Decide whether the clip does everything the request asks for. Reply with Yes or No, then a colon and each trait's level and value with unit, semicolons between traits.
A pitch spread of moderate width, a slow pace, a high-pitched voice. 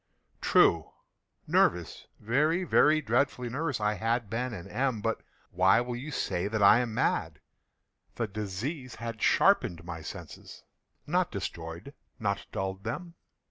No: average, 4.8 semitones; slow, 120 wpm; low, 115 Hz